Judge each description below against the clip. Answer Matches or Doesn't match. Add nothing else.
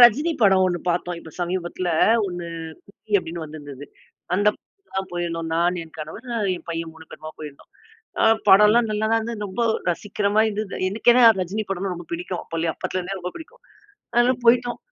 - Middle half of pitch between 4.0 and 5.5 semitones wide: Matches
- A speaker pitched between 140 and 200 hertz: Matches